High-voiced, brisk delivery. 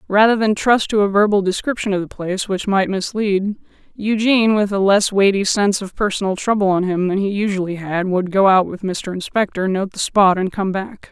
Yes: high, 200 Hz; fast, 215 wpm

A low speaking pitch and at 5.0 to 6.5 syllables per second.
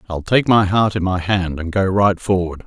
No: very low, 95 Hz; 4.8 syllables/s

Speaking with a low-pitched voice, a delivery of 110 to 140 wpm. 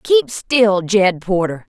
No: high, 200 Hz; slow, 135 wpm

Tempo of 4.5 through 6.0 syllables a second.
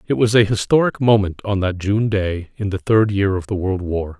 Yes: 5.0 syllables/s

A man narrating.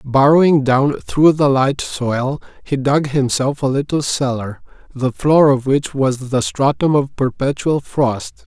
Yes: male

